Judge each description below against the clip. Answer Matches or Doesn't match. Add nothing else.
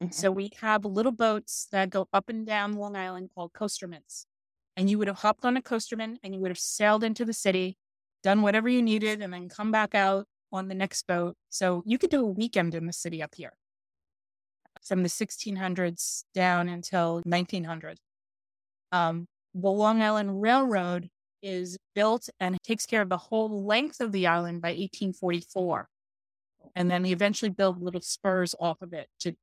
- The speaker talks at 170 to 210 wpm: Matches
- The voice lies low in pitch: Doesn't match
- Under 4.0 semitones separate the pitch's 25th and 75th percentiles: Matches